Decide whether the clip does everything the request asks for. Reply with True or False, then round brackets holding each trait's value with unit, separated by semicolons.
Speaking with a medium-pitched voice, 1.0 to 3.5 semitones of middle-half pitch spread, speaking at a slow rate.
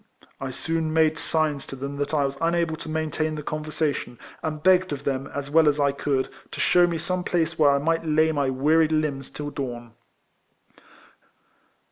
False (155 Hz; 2.4 semitones; 185 wpm)